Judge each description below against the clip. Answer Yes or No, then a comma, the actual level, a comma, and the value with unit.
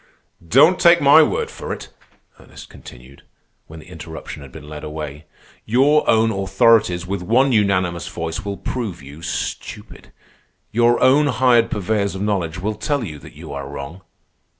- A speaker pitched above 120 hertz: No, low, 100 Hz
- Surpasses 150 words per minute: Yes, average, 160 wpm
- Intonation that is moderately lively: No, wide, 6.7 semitones